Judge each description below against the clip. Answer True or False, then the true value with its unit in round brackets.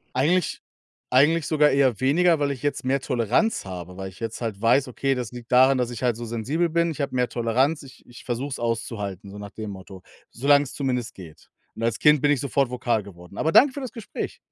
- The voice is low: True (125 Hz)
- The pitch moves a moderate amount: True (4.1 semitones)